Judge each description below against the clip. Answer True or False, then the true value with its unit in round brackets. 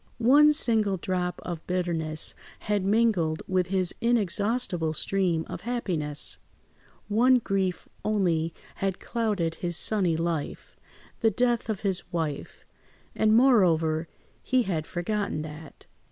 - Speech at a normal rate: False (110 wpm)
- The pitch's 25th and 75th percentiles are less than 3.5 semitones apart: False (4.9 semitones)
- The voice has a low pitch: False (185 Hz)